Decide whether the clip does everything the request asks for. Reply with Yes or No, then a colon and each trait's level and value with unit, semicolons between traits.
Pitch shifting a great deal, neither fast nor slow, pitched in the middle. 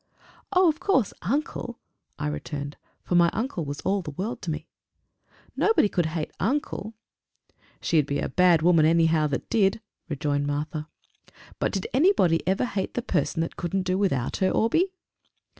Yes: wide, 6.4 semitones; average, 160 wpm; medium, 180 Hz